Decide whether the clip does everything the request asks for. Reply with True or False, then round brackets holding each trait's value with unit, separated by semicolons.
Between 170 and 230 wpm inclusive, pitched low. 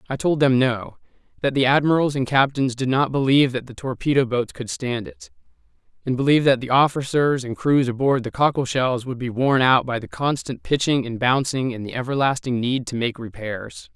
True (200 wpm; 130 Hz)